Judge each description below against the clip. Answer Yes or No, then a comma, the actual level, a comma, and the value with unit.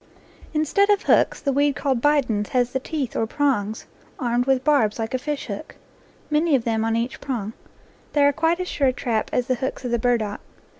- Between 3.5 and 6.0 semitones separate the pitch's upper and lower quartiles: Yes, average, 3.9 semitones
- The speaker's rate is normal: No, fast, 210 wpm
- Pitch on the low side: No, very high, 255 Hz